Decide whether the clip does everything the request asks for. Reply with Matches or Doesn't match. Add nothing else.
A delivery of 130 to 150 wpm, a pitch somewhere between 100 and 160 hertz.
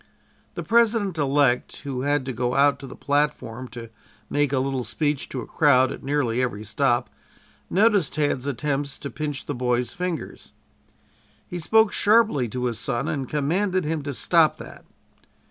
Doesn't match